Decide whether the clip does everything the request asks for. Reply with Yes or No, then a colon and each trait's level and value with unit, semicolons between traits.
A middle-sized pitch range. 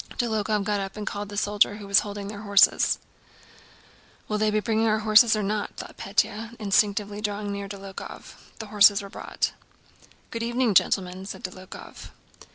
No: narrow, 1.3 semitones